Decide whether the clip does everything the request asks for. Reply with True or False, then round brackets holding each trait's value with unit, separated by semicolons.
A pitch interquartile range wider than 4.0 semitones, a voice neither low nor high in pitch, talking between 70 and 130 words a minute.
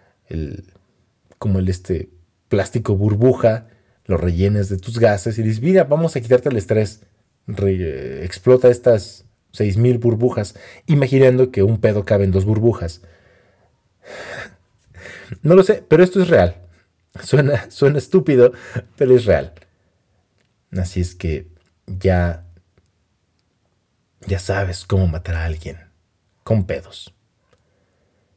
False (4.4 semitones; 100 Hz; 125 wpm)